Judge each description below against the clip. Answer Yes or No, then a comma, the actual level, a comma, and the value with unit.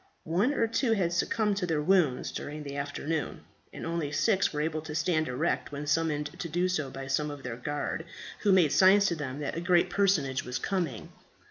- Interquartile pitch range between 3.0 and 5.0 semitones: Yes, average, 4.0 semitones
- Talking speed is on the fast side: Yes, fast, 210 wpm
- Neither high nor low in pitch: Yes, medium, 155 Hz